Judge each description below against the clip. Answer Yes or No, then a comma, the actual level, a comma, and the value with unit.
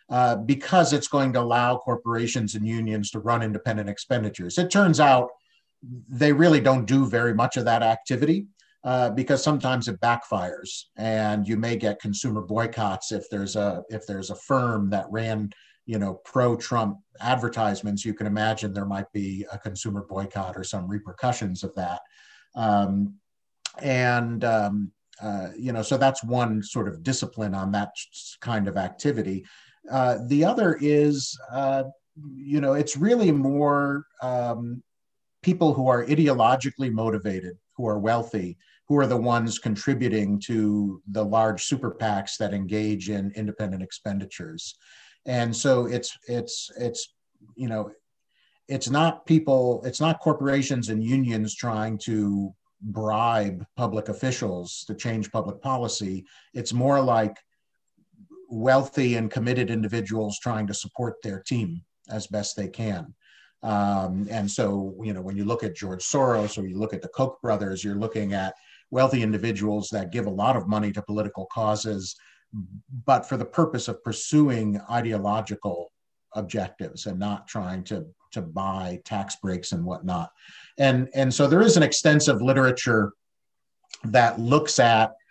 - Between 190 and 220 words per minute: No, average, 150 wpm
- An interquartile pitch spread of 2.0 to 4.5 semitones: Yes, average, 4.0 semitones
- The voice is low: Yes, low, 115 Hz